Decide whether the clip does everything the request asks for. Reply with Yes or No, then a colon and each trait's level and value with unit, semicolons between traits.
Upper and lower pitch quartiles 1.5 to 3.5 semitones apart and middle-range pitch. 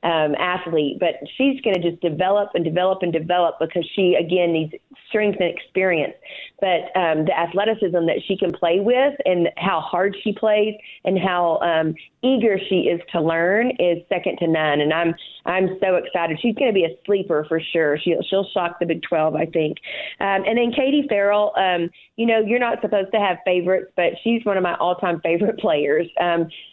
Yes: average, 3.2 semitones; medium, 180 Hz